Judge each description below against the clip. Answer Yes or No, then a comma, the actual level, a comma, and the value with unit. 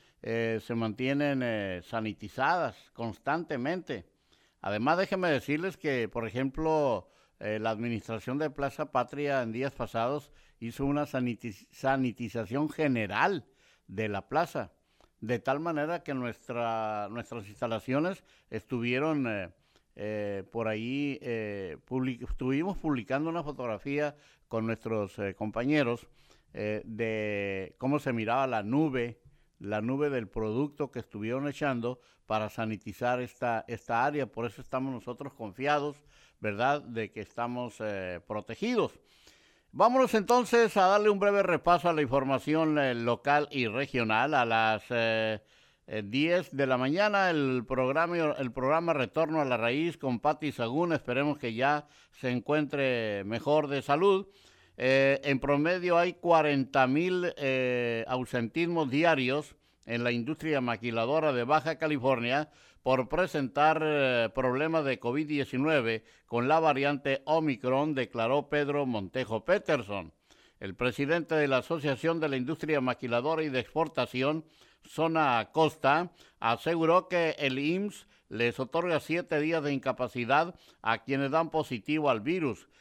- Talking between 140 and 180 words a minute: No, average, 130 wpm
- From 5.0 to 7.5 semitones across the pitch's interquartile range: No, average, 4.6 semitones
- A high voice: No, low, 135 Hz